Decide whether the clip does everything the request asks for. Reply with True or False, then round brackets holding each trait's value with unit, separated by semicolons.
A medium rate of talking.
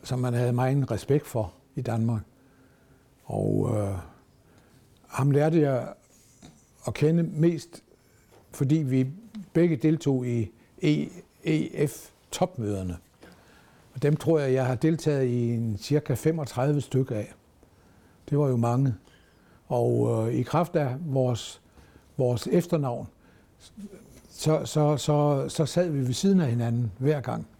False (125 wpm)